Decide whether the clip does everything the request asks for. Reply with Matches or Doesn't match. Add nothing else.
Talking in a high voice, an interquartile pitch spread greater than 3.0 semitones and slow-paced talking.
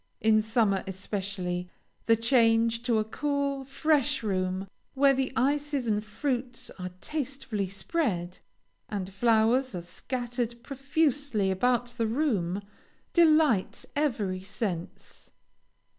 Matches